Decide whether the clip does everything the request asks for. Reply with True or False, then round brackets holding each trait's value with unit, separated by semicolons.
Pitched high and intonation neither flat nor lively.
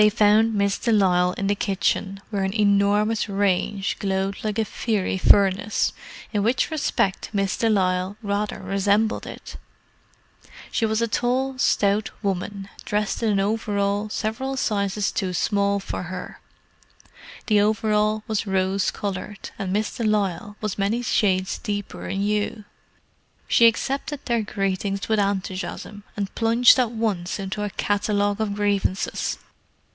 False (205 Hz; 1.7 semitones)